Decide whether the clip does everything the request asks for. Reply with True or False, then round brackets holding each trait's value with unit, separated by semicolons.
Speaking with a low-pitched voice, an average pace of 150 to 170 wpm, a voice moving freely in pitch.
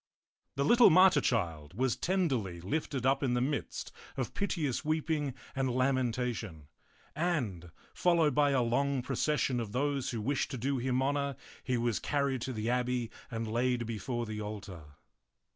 False (130 Hz; 160 wpm; 3.6 semitones)